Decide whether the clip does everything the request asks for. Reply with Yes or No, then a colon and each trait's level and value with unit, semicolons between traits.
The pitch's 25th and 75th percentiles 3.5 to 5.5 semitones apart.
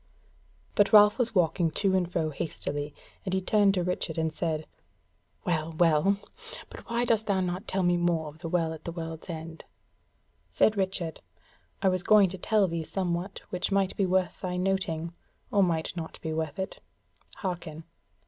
No: average, 3.0 semitones